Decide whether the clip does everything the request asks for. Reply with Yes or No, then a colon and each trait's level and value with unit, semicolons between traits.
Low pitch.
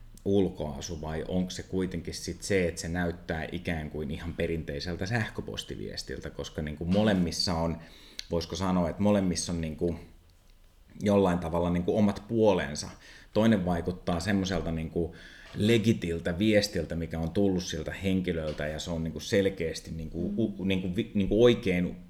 Yes: very low, 90 Hz